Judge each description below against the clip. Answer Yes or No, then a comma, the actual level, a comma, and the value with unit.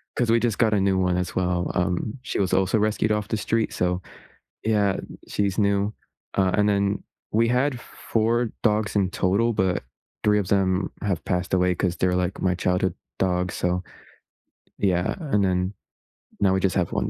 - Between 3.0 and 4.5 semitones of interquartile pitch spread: No, narrow, 2.6 semitones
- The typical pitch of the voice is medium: No, very low, 95 Hz